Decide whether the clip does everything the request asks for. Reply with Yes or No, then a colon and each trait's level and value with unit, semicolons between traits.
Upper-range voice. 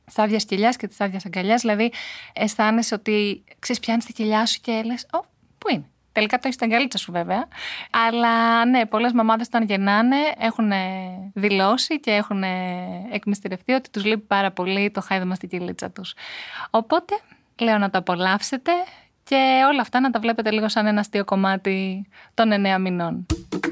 Yes: high, 215 Hz